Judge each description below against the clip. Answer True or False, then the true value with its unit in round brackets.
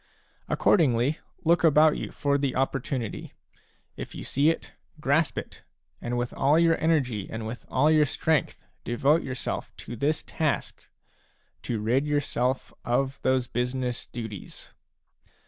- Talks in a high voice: False (135 Hz)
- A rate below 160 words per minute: True (140 wpm)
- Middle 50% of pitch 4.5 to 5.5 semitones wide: False (3.7 semitones)